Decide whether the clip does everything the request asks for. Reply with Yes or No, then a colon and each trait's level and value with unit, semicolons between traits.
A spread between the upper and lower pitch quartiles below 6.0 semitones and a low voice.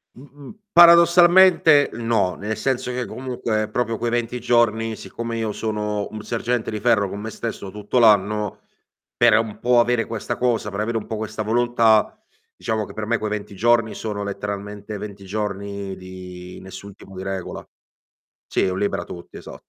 Yes: average, 2.7 semitones; low, 110 Hz